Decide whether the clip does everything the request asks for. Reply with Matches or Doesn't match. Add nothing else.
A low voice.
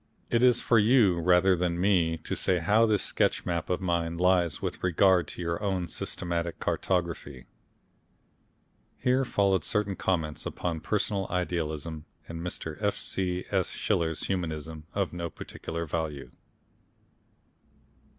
Matches